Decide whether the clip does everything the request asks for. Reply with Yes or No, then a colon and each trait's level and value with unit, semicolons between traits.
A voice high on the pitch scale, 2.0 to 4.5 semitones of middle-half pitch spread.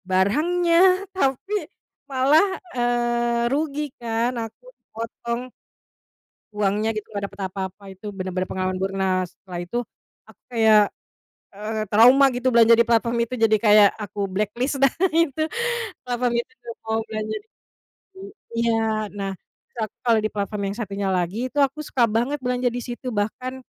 Yes: high, 225 Hz; average, 3.4 semitones